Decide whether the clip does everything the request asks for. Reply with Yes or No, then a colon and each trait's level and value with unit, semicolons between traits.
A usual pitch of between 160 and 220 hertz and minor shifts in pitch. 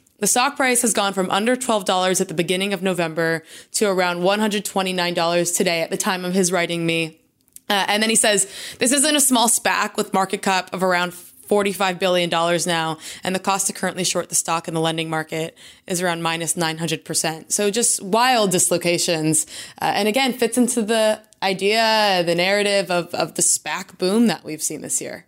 No: high, 190 Hz; average, 3.5 semitones